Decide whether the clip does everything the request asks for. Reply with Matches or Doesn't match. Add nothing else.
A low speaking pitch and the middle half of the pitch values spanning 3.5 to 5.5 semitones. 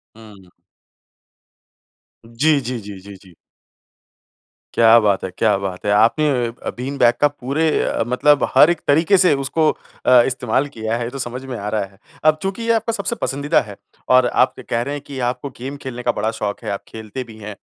Matches